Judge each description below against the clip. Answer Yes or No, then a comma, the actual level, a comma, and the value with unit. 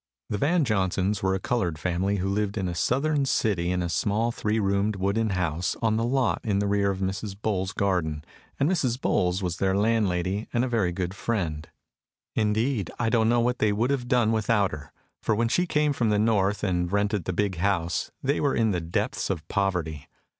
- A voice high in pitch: No, low, 100 Hz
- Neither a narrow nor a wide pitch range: Yes, average, 3.8 semitones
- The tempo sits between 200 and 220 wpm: Yes, fast, 205 wpm